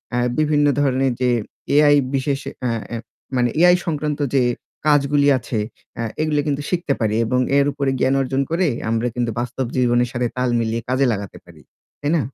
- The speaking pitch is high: No, low, 135 Hz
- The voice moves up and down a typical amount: Yes, average, 3.1 semitones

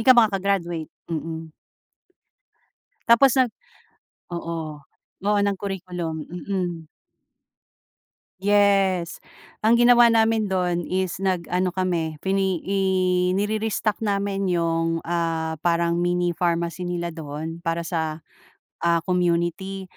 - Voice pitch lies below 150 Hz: No, medium, 180 Hz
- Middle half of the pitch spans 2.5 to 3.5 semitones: Yes, average, 2.9 semitones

